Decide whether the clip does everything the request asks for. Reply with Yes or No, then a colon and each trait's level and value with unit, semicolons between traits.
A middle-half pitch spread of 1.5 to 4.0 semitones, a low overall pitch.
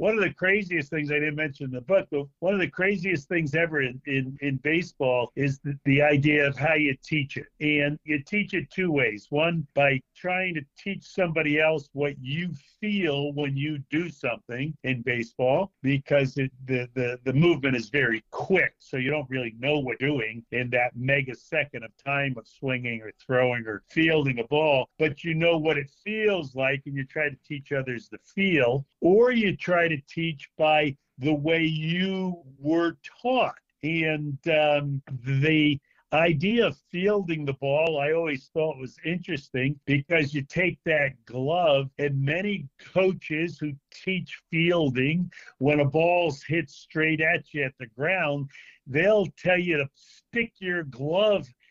No: average, 3.6 semitones; medium, 150 Hz